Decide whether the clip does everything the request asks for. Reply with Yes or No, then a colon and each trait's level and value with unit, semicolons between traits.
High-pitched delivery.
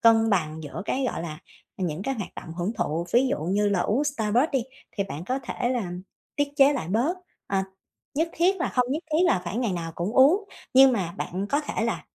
Yes: high, 225 Hz